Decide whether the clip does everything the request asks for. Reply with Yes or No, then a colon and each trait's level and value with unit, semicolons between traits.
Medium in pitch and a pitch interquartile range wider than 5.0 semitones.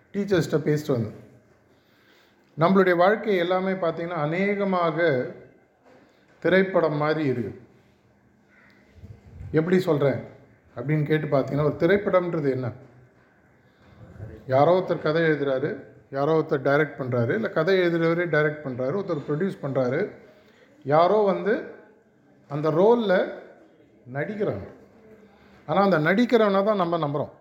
Yes: medium, 155 Hz; wide, 5.4 semitones